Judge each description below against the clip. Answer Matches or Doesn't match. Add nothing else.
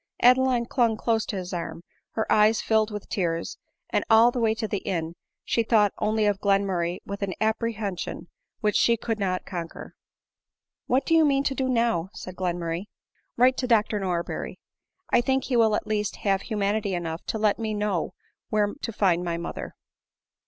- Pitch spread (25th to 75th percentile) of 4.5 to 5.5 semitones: Doesn't match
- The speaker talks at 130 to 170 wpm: Doesn't match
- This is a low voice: Doesn't match